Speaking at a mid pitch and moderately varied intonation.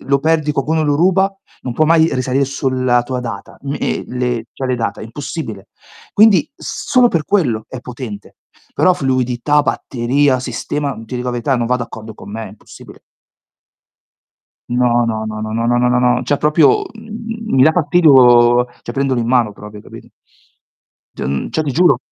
No: low, 130 Hz; average, 3.9 semitones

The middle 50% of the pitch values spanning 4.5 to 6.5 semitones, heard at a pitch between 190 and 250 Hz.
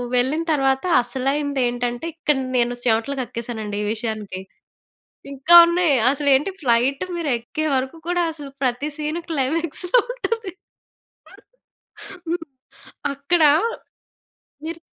No: average, 5.0 semitones; very high, 275 Hz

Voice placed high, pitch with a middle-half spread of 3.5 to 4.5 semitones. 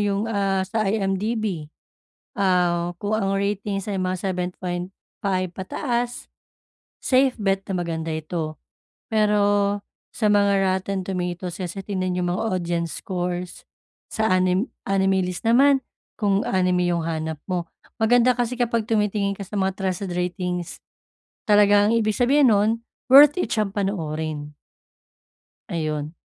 No: high, 195 Hz; average, 2.9 semitones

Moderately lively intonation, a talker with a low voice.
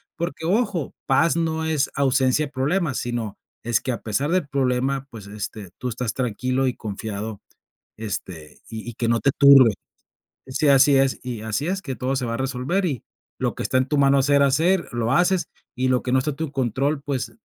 Yes: average, 3.7 semitones; low, 130 Hz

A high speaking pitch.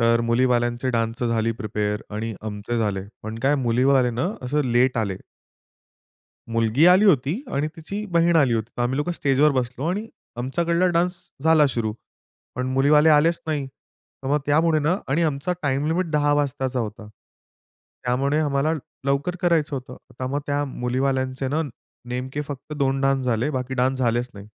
No: low, 135 Hz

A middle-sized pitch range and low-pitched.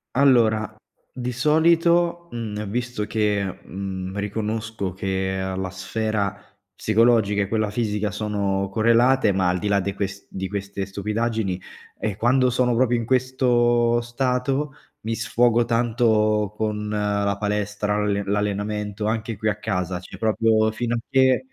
Yes: average, 3.0 semitones; low, 110 Hz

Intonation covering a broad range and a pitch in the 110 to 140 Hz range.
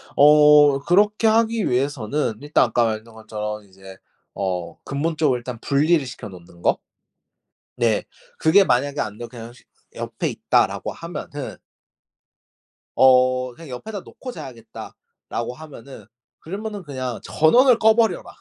Yes: wide, 5.7 semitones; low, 135 Hz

